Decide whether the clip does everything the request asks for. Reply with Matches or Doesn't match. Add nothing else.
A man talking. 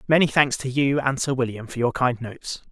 Matches